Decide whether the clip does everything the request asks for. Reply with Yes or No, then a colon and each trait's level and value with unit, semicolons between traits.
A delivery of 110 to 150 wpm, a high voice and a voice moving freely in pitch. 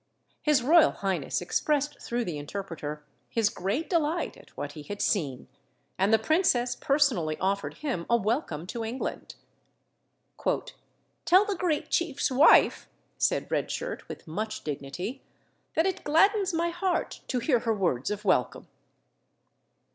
Yes: average, 140 wpm; high, 235 Hz; wide, 9.0 semitones